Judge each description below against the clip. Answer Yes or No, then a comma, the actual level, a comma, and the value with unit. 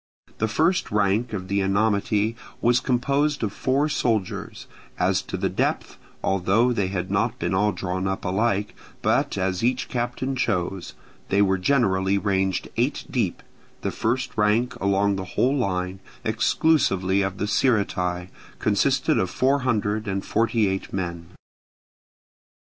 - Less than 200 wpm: Yes, average, 140 wpm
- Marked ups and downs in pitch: No, average, 4.1 semitones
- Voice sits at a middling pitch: No, low, 105 Hz